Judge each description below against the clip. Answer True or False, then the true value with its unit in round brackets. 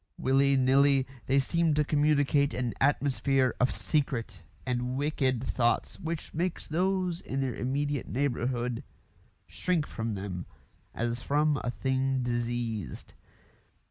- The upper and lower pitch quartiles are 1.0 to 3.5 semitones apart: True (3.1 semitones)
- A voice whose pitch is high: False (135 Hz)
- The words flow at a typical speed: False (120 wpm)